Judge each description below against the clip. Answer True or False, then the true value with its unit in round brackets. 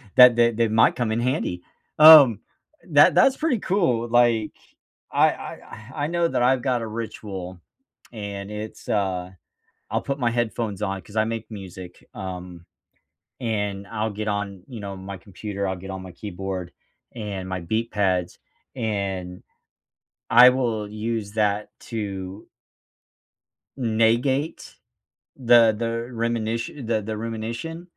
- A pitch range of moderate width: True (3.3 semitones)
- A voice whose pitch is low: True (110 Hz)